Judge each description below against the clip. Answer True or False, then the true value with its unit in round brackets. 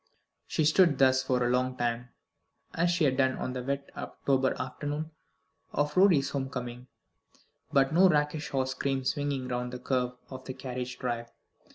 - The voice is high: False (130 Hz)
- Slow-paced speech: False (170 wpm)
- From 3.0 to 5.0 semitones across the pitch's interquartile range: False (2.5 semitones)